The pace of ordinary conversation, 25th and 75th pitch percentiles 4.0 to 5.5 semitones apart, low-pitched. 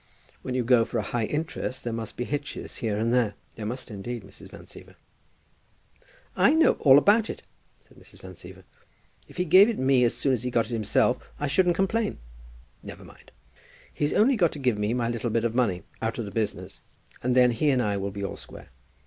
No: fast, 215 wpm; average, 4.5 semitones; low, 125 Hz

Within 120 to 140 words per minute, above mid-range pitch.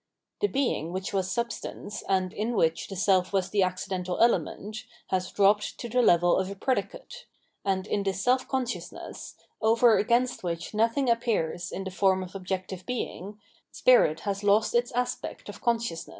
No: average, 170 wpm; high, 200 Hz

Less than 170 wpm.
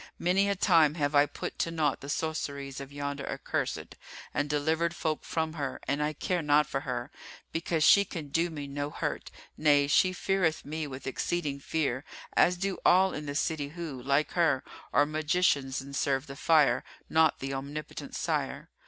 No: average, 180 wpm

